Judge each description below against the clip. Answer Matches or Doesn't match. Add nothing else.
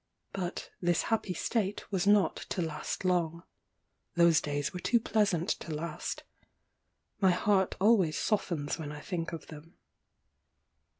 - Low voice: Doesn't match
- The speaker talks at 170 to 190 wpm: Doesn't match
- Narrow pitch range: Doesn't match